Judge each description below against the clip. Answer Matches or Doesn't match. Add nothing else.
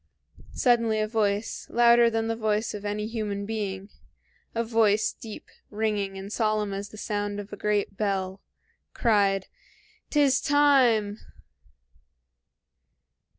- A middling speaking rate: Doesn't match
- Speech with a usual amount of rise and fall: Doesn't match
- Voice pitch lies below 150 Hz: Doesn't match